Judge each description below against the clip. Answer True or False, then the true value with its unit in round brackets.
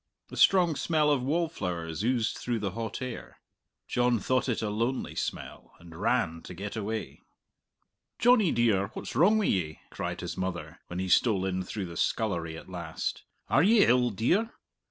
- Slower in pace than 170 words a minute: False (175 wpm)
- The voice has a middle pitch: False (110 Hz)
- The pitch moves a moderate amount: False (6.0 semitones)